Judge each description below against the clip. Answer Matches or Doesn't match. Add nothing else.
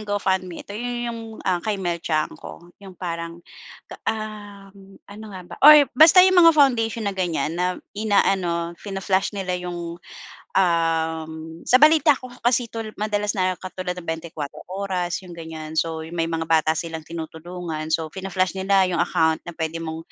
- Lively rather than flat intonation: Doesn't match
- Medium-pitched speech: Matches